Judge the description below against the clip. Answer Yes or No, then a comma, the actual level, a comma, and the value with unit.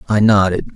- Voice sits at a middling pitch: No, low, 100 Hz